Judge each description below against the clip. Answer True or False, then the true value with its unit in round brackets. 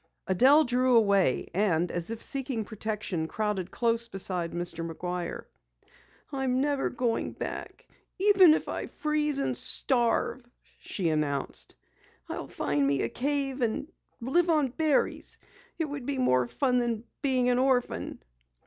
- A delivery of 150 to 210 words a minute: False (140 wpm)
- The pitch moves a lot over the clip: True (6.8 semitones)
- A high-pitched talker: True (240 Hz)